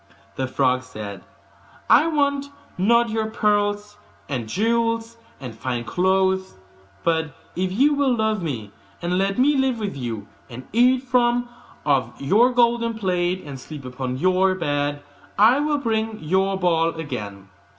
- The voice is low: No, high, 190 Hz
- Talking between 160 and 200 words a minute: No, average, 150 wpm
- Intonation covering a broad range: Yes, wide, 8.8 semitones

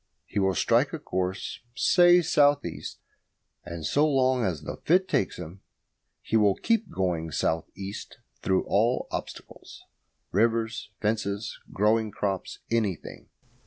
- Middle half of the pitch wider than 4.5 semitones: Yes, average, 5.3 semitones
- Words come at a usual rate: No, slow, 130 wpm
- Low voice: Yes, low, 105 Hz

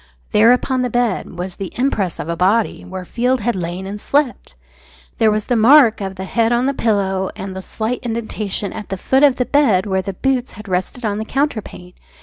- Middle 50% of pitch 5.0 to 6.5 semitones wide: No, average, 4.5 semitones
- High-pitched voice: Yes, high, 215 Hz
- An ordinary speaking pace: No, fast, 215 wpm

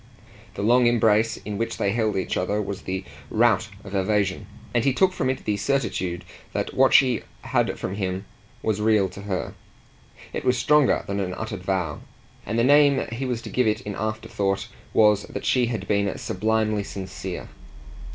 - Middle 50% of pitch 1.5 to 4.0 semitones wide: Yes, average, 3.4 semitones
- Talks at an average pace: Yes, average, 180 wpm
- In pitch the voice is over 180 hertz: No, low, 105 Hz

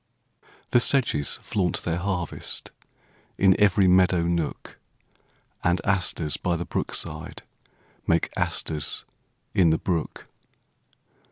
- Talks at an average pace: No, slow, 105 wpm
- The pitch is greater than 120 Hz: No, very low, 90 Hz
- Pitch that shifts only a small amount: Yes, narrow, 2.2 semitones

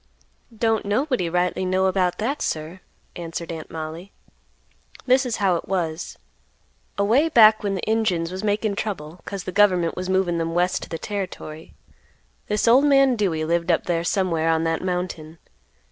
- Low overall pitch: No, medium, 185 Hz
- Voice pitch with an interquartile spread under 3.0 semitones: No, average, 4.0 semitones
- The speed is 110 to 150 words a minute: No, average, 165 wpm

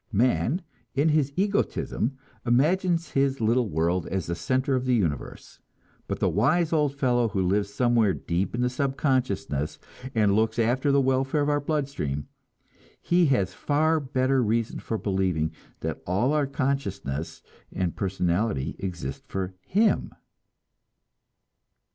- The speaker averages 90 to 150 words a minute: Yes, average, 140 wpm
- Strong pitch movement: Yes, wide, 6.4 semitones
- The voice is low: Yes, low, 120 Hz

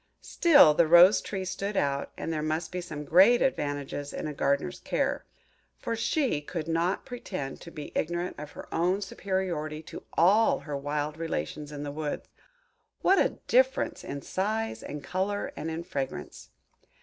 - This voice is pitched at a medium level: Yes, medium, 165 Hz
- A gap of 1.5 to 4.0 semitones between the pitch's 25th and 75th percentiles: No, average, 4.5 semitones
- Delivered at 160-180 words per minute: Yes, average, 165 wpm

